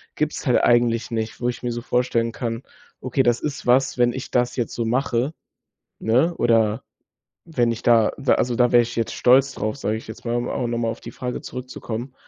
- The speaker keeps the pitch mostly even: Yes, narrow, 1.5 semitones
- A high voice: No, low, 120 Hz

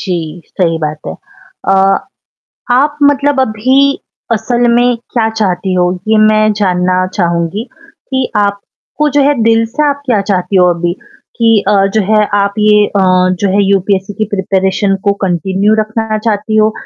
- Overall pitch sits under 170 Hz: No, high, 210 Hz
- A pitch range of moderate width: Yes, average, 3.2 semitones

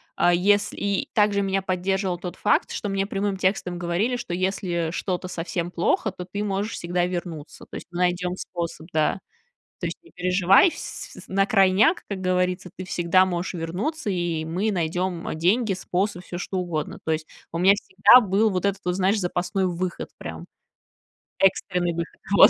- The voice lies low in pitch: No, medium, 185 Hz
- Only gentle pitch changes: Yes, narrow, 2.1 semitones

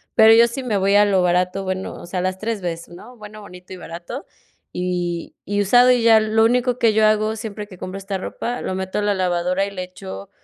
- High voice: Yes, high, 200 Hz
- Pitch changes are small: No, average, 3.3 semitones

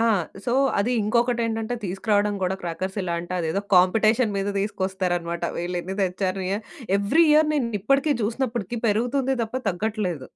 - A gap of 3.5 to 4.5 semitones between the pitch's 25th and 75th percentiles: Yes, average, 4.2 semitones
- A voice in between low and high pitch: No, high, 205 Hz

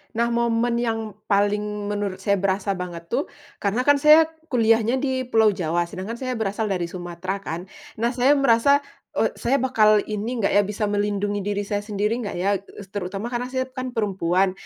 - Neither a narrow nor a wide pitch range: Yes, average, 3.3 semitones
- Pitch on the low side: No, high, 210 Hz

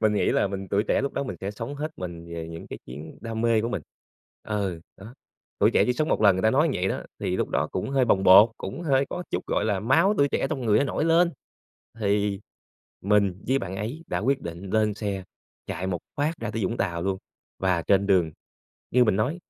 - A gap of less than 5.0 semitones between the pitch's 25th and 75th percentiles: No, wide, 5.4 semitones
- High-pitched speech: No, low, 105 Hz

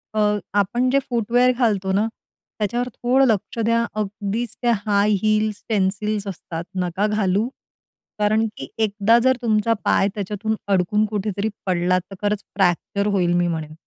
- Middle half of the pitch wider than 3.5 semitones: No, narrow, 2.4 semitones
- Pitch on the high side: Yes, high, 210 Hz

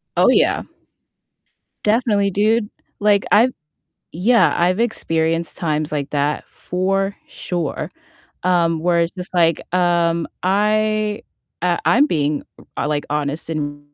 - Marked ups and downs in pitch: No, average, 4.4 semitones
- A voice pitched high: No, medium, 175 Hz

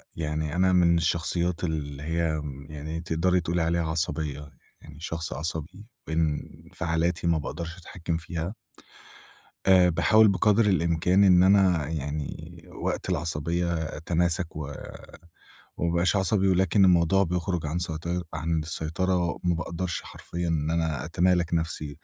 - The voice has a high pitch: No, very low, 85 Hz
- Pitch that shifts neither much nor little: No, narrow, 2.0 semitones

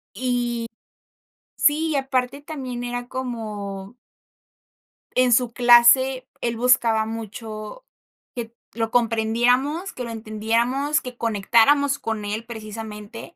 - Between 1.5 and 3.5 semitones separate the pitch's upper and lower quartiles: Yes, narrow, 2.5 semitones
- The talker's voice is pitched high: Yes, high, 240 Hz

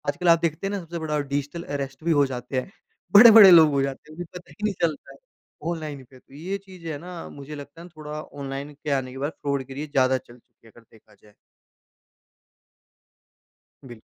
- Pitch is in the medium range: Yes, medium, 145 Hz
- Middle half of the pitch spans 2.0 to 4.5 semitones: Yes, average, 3.7 semitones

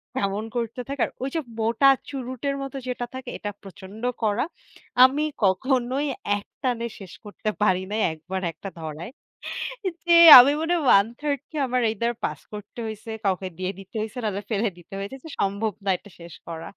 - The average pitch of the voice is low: No, high, 220 Hz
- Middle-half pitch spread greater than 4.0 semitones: Yes, average, 4.7 semitones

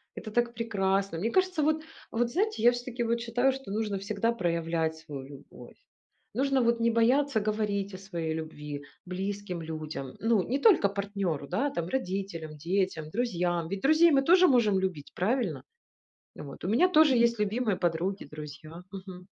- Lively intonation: Yes, wide, 5.8 semitones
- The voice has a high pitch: Yes, high, 200 Hz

